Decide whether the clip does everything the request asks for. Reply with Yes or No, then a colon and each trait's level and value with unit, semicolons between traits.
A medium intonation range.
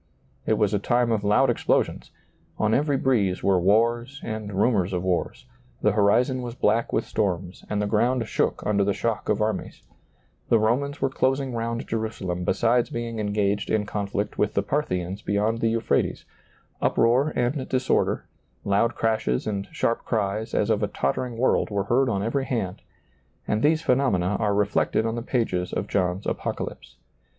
Yes: average, 3.1 semitones